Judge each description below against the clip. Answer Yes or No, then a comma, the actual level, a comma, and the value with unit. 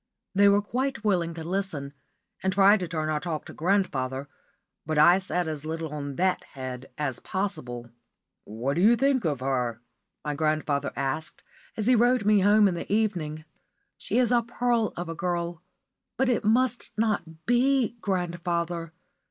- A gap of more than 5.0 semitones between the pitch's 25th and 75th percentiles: Yes, wide, 5.6 semitones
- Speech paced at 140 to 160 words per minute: No, average, 170 wpm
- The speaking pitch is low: No, medium, 175 Hz